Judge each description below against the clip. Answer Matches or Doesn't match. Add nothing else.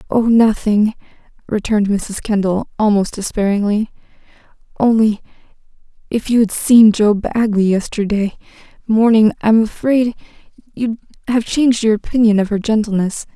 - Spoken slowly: Matches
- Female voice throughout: Matches